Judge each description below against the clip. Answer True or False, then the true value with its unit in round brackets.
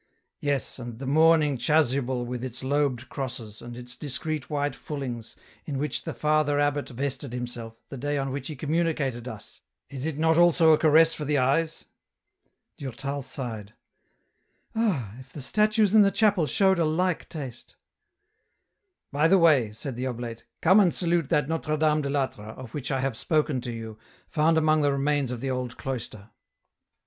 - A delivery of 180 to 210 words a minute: True (190 wpm)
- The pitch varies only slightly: False (4.0 semitones)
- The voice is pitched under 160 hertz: True (140 Hz)